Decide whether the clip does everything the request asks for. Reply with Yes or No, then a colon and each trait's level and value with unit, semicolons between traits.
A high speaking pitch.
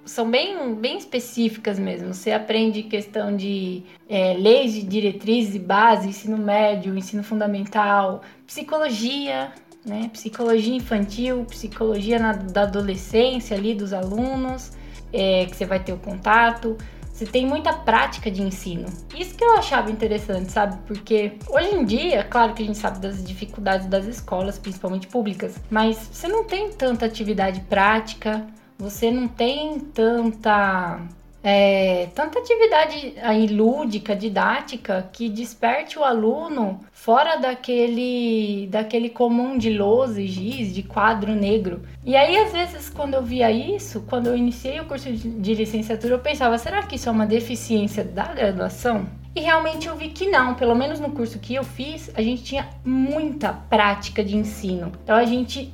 Yes: high, 220 Hz